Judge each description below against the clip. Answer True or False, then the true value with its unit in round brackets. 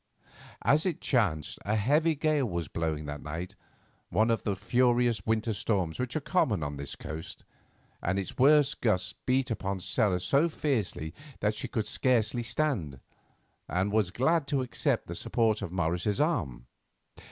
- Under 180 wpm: True (160 wpm)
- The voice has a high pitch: False (110 Hz)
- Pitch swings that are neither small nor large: False (6.7 semitones)